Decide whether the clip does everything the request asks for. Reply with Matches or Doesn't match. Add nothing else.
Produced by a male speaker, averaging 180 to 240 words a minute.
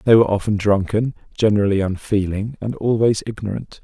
Doesn't match